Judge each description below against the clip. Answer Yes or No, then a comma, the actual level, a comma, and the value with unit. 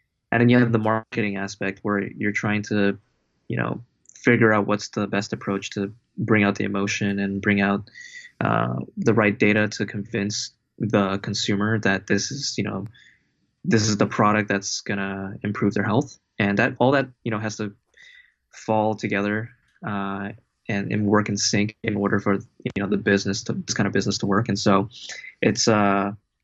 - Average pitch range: No, narrow, 1.8 semitones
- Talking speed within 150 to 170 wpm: No, average, 190 wpm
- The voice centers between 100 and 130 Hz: Yes, low, 105 Hz